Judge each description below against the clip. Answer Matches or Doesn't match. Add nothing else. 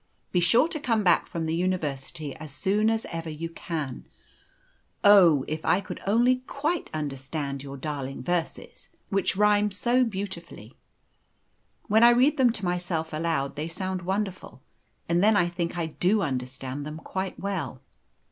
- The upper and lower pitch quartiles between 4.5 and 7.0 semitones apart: Matches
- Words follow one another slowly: Doesn't match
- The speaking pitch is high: Doesn't match